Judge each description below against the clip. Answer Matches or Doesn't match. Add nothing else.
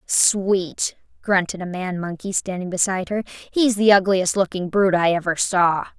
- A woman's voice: Matches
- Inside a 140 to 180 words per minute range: Matches